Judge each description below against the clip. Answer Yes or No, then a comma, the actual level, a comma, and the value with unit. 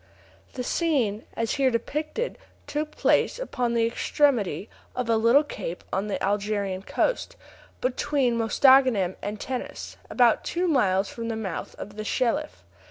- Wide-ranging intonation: No, average, 4.7 semitones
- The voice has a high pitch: Yes, high, 230 Hz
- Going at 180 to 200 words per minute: No, average, 145 wpm